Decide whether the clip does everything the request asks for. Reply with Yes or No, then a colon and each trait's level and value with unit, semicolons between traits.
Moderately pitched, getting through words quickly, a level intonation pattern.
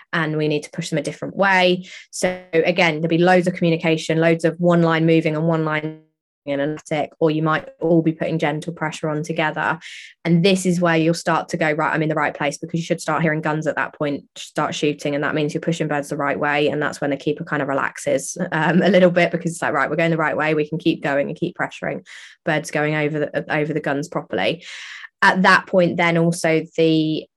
Yes: medium, 160 Hz; fast, 250 wpm; narrow, 1.8 semitones